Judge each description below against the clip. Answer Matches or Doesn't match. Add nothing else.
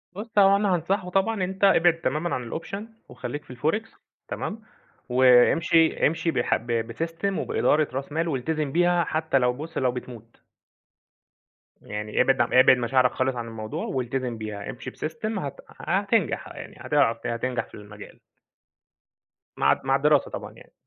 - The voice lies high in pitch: Doesn't match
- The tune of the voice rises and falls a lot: Matches